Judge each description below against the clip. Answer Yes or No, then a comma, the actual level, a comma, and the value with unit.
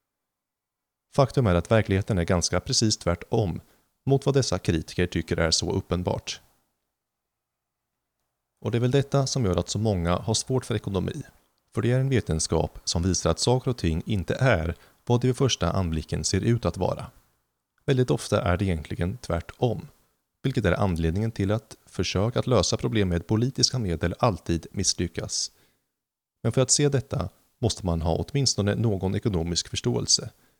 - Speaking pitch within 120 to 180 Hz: No, low, 100 Hz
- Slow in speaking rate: No, average, 165 wpm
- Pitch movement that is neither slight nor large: No, wide, 6.2 semitones